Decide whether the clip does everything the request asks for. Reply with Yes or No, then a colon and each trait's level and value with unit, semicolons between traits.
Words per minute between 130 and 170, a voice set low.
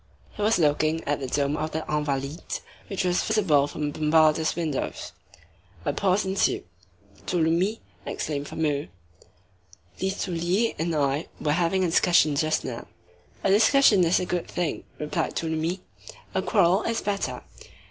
No: average, 140 wpm; medium, 165 Hz